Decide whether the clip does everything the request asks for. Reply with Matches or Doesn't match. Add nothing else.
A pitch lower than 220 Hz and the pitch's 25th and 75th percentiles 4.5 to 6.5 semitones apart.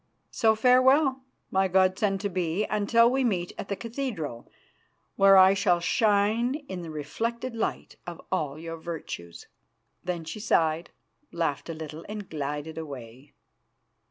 Matches